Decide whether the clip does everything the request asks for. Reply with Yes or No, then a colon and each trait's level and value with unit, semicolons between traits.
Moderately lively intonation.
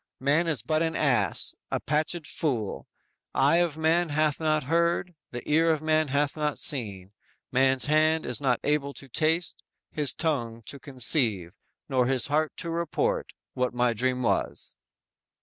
Yes: average, 3.9 semitones